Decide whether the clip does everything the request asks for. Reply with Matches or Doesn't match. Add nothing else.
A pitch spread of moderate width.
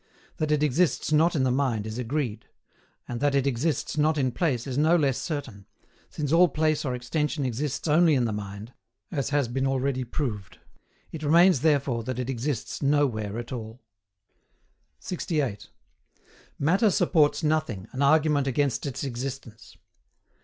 Matches